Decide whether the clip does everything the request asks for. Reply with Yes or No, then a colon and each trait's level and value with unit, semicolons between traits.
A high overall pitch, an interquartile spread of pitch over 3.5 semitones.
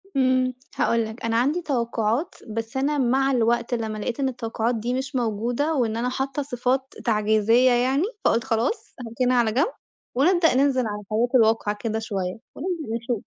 No: high, 240 Hz; average, 3.0 semitones